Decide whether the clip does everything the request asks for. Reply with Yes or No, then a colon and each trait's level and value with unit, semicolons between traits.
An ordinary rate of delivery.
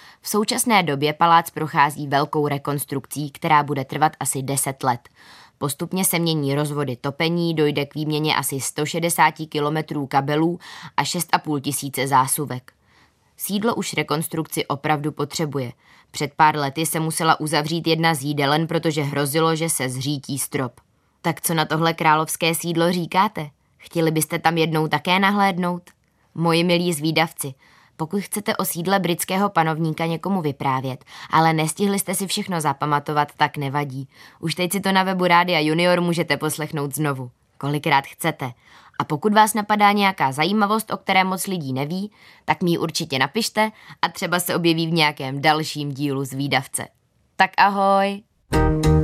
Yes: average, 150 wpm